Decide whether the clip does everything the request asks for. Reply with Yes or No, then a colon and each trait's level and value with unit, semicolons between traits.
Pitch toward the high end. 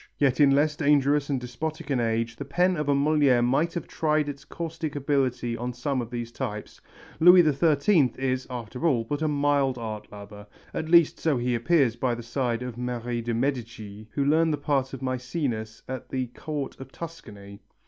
No: low, 135 Hz